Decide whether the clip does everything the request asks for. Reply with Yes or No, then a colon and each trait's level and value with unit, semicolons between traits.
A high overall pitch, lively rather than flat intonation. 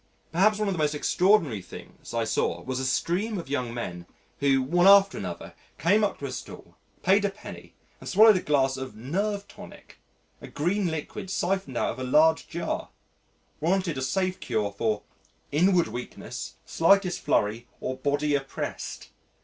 No: medium, 150 Hz; wide, 6.8 semitones